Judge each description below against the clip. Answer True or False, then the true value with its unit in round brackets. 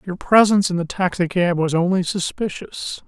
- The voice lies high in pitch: False (180 Hz)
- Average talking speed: True (155 wpm)